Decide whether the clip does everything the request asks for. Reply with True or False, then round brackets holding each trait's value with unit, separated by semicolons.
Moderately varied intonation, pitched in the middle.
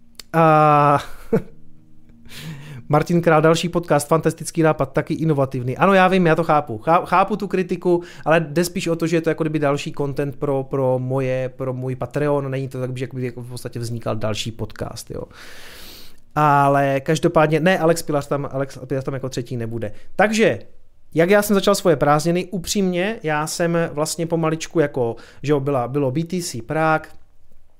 True (4.4 semitones; 150 Hz)